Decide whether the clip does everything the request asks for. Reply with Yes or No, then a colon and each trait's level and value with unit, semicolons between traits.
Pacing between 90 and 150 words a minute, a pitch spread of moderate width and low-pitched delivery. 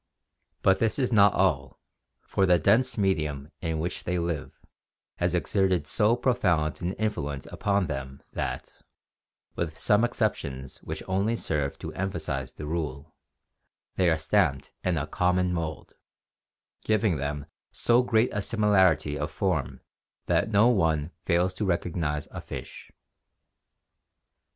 Yes: slow, 135 wpm; average, 4.9 semitones; very low, 90 Hz